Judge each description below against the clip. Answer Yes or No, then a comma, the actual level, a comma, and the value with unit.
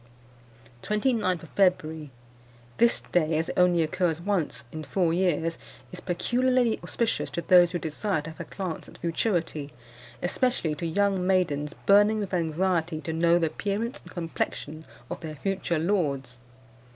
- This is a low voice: No, medium, 175 Hz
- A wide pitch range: No, average, 3.7 semitones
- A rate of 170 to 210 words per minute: No, average, 155 wpm